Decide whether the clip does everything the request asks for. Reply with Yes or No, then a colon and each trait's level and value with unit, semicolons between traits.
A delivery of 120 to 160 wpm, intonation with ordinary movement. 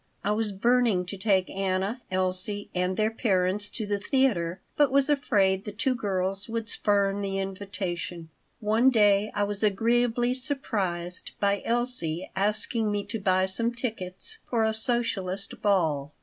Yes: average, 150 wpm; average, 3.4 semitones